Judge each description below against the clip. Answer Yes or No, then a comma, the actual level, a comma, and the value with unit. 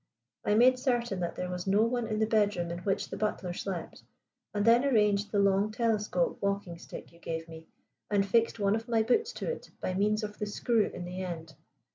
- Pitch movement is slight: No, average, 3.7 semitones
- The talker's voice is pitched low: No, high, 205 Hz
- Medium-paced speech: No, fast, 215 wpm